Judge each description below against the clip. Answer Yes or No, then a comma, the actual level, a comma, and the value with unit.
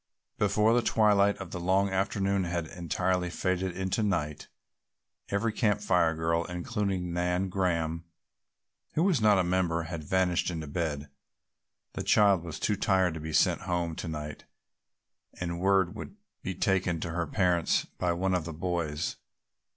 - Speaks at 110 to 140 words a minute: No, average, 160 wpm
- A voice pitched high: No, very low, 90 Hz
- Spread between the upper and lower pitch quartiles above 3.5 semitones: No, narrow, 2.6 semitones